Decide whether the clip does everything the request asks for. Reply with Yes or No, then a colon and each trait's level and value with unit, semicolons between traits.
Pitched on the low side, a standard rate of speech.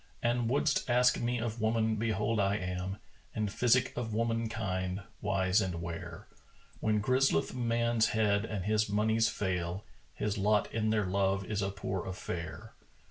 Yes: low, 105 Hz; average, 160 wpm